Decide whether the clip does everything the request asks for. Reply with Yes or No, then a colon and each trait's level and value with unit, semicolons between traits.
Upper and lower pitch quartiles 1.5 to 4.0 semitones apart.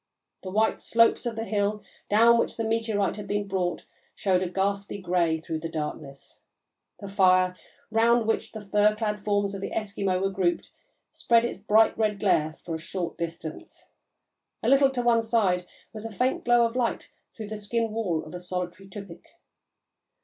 Yes: average, 3.5 semitones